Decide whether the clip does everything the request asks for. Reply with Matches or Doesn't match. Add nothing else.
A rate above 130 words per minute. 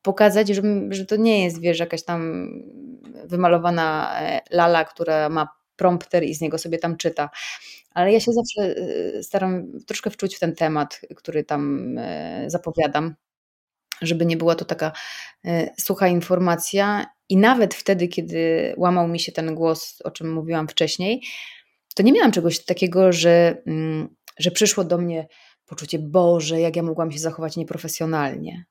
Matches